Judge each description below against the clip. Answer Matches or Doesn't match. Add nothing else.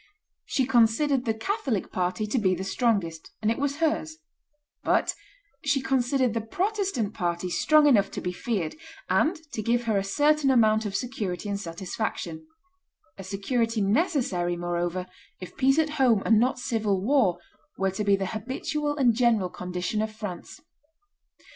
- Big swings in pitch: Matches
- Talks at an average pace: Matches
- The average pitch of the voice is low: Doesn't match